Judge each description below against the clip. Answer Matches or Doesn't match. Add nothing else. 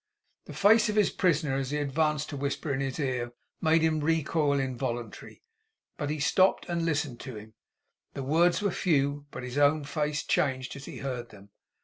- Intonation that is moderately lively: Matches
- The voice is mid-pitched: Matches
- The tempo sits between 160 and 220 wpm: Matches